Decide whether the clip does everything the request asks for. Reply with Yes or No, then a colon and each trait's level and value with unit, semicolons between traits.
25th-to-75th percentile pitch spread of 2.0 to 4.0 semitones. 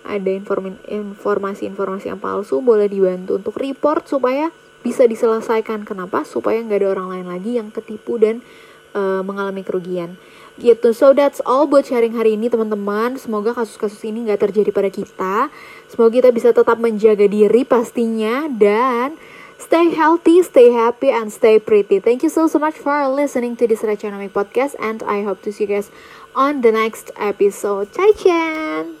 No: average, 4.5 semitones